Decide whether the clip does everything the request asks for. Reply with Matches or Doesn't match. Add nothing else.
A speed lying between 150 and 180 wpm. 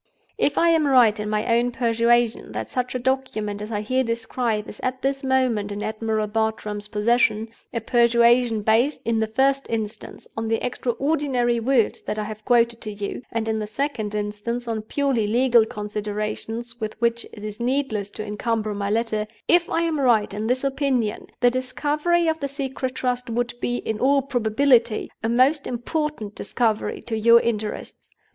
Matches